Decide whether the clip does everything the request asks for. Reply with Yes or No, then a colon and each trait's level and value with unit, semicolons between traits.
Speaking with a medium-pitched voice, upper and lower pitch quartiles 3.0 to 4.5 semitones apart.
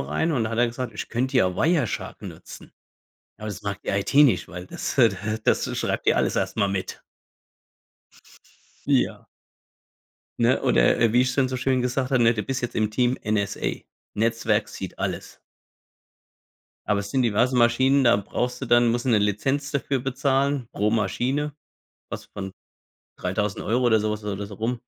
No: low, 115 Hz; average, 3.8 semitones